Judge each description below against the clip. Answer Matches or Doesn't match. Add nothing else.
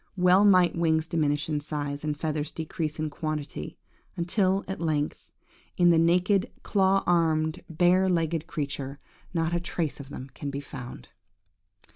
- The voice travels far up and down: Doesn't match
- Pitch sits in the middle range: Matches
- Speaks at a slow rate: Doesn't match